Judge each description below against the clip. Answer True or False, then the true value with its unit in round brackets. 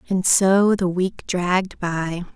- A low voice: False (185 Hz)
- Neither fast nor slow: True (155 wpm)